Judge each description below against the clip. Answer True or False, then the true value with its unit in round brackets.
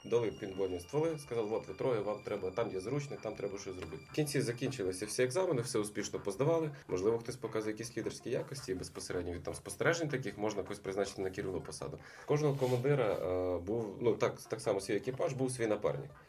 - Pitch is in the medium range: False (115 Hz)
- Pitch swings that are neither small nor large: False (5.7 semitones)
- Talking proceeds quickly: True (200 wpm)